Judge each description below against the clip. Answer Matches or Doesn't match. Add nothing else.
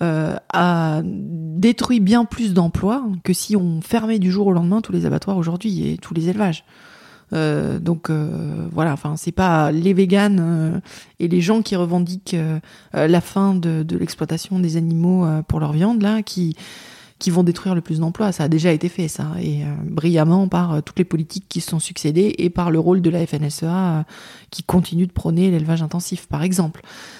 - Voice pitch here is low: Doesn't match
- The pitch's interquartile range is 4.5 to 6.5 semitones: Doesn't match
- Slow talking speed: Doesn't match